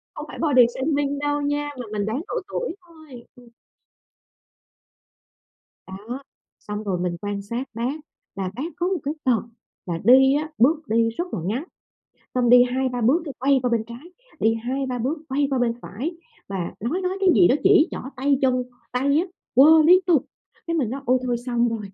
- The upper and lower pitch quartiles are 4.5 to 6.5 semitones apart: No, average, 4.0 semitones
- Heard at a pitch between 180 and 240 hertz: No, very high, 255 Hz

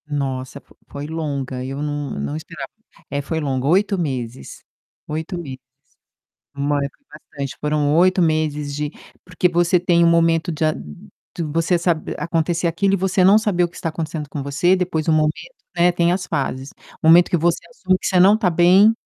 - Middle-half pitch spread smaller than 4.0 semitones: Yes, average, 3.5 semitones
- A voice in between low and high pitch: Yes, medium, 160 Hz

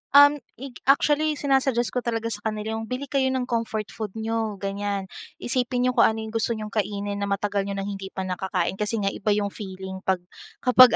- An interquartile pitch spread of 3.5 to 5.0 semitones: Yes, average, 3.8 semitones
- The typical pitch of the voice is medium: No, high, 220 Hz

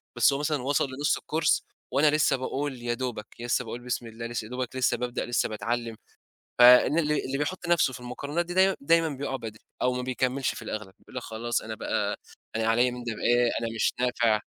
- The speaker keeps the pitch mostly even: No, average, 3.2 semitones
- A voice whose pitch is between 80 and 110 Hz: No, low, 125 Hz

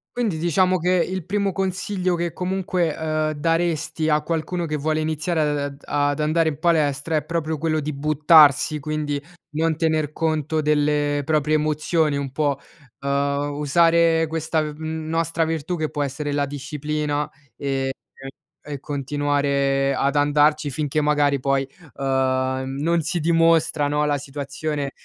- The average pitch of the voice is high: No, medium, 150 Hz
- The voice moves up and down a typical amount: No, narrow, 2.2 semitones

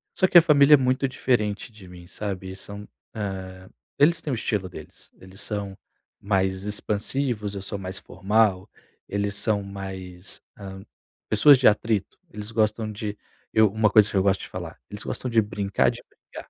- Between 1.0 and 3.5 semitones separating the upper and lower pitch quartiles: Yes, narrow, 2.5 semitones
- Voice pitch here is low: Yes, low, 105 Hz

